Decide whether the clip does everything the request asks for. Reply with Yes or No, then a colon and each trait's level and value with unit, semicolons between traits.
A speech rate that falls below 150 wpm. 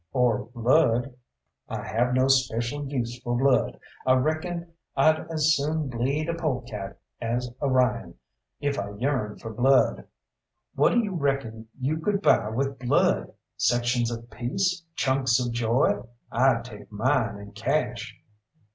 Yes: average, 140 wpm